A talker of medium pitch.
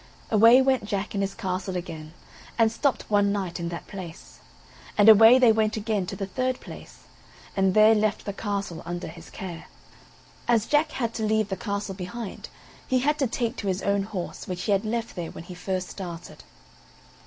No: high, 205 Hz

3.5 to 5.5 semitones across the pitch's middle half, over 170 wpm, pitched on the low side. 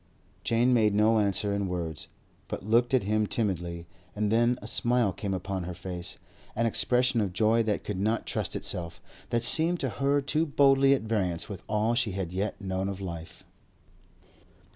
Yes: average, 3.9 semitones; average, 180 wpm; low, 105 Hz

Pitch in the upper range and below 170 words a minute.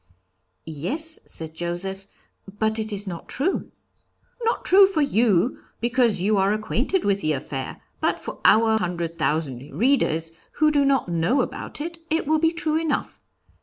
Yes: high, 220 Hz; average, 160 wpm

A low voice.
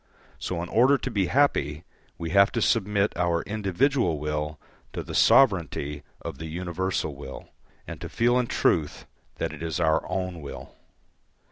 Yes: very low, 90 Hz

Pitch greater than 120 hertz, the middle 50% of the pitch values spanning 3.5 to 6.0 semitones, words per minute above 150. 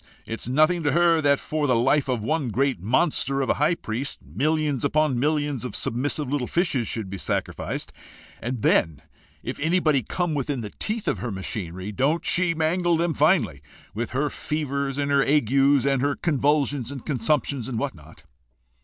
Yes: medium, 140 Hz; average, 4.1 semitones; average, 180 wpm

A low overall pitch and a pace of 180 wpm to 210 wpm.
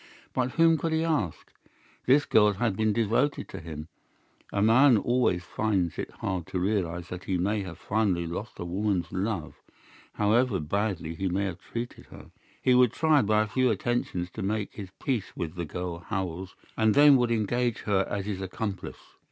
Yes: low, 105 Hz; average, 185 wpm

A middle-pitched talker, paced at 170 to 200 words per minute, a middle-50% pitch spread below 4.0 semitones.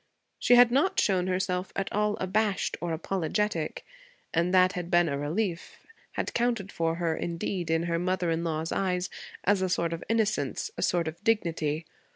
Yes: medium, 180 Hz; average, 180 wpm; average, 3.2 semitones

